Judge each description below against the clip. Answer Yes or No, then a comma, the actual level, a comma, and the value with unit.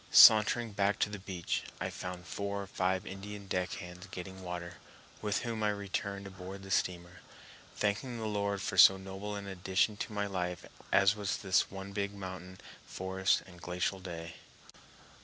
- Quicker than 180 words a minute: No, average, 170 wpm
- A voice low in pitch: Yes, very low, 95 Hz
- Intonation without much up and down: Yes, narrow, 1.7 semitones